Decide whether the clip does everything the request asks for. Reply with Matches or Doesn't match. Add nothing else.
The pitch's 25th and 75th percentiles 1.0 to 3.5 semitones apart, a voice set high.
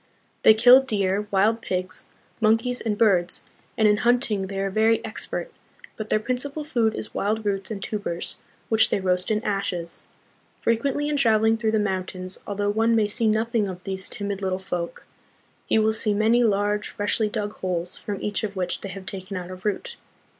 Matches